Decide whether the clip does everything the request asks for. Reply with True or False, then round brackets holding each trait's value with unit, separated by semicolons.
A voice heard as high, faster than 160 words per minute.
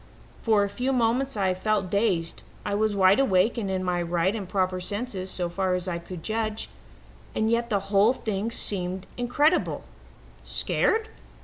True (200 Hz; 170 wpm)